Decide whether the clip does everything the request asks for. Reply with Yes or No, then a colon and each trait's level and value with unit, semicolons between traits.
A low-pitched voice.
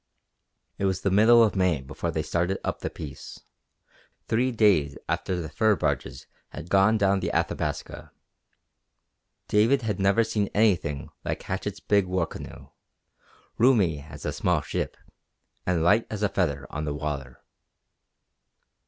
Yes: very low, 95 Hz